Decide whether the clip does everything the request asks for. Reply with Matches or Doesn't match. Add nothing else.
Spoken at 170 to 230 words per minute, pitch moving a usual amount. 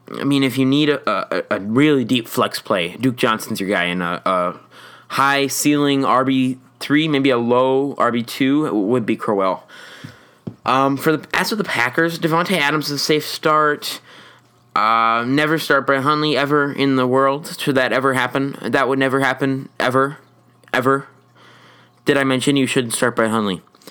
Doesn't match